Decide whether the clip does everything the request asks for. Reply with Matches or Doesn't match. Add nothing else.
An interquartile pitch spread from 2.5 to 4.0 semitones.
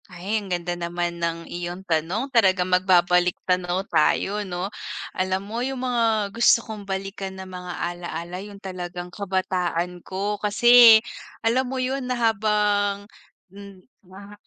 Matches